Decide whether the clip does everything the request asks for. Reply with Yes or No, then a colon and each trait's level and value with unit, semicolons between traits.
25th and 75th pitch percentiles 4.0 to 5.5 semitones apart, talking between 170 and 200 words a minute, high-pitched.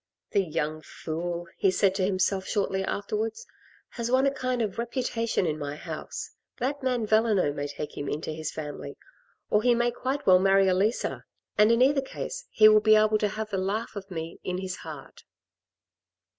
Yes: average, 4.4 semitones; average, 185 wpm; high, 200 Hz